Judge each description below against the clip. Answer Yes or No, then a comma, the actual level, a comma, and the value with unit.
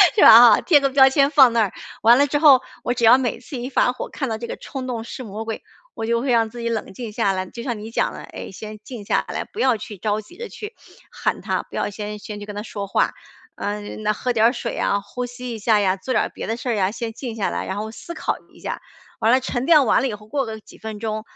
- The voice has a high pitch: Yes, high, 230 Hz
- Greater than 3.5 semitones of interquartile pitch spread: No, average, 3.1 semitones